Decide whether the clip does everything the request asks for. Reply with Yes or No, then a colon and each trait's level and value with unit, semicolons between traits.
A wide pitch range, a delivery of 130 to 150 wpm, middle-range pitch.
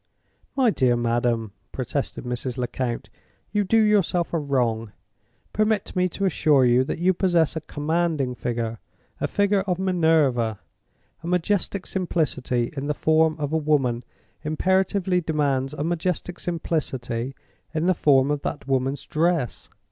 Yes: wide, 5.7 semitones; average, 140 wpm; medium, 155 Hz